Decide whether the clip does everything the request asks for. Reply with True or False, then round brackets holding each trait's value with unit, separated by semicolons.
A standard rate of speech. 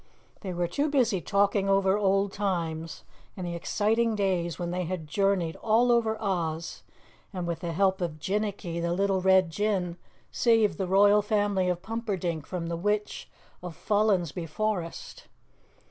True (155 wpm)